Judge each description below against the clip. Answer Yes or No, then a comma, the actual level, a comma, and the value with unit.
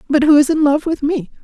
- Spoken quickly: Yes, fast, 290 wpm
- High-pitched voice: Yes, very high, 295 Hz